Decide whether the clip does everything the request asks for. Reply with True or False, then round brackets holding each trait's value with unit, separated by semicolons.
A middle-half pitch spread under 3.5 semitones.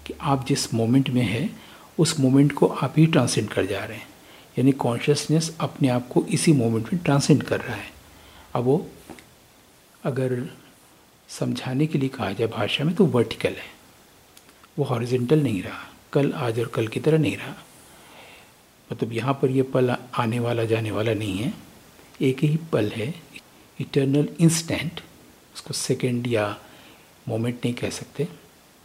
False (4.3 semitones)